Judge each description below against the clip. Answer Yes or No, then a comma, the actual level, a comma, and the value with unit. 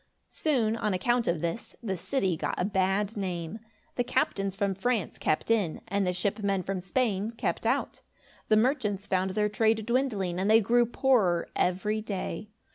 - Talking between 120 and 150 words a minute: No, average, 175 wpm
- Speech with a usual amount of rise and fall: Yes, average, 3.2 semitones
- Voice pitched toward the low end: No, high, 205 Hz